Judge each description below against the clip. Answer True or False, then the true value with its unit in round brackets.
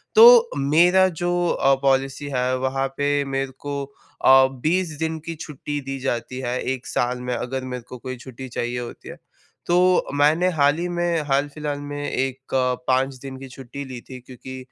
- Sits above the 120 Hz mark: True (135 Hz)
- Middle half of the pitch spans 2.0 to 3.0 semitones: True (2.5 semitones)